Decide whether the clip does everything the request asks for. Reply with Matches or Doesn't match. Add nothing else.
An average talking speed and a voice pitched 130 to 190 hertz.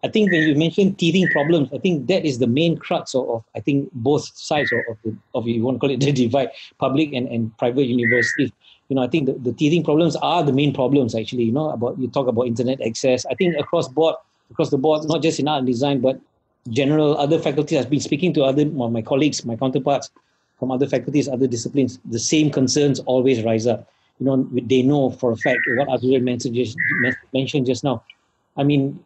Doesn't match